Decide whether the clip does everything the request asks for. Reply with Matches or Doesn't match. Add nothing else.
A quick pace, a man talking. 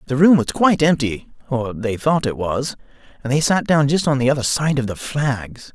Matches